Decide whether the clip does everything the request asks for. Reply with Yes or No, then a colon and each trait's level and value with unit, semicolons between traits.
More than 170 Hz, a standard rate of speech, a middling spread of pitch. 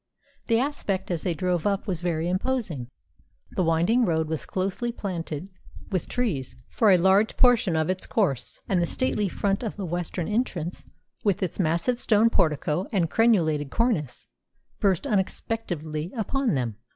Yes: medium, 185 Hz; average, 155 wpm; average, 5.0 semitones